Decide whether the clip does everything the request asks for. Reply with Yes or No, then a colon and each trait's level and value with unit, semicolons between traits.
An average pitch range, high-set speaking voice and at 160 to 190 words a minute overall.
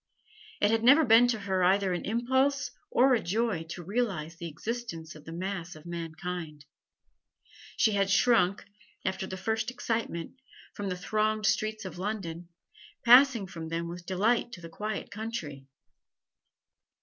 No: average, 4.9 semitones; high, 195 Hz; average, 150 wpm